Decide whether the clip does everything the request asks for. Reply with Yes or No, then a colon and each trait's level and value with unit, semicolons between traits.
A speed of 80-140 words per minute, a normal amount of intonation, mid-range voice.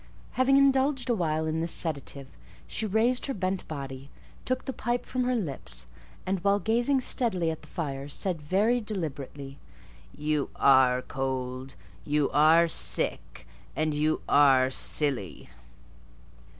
No: slow, 135 wpm; wide, 8.0 semitones; medium, 160 Hz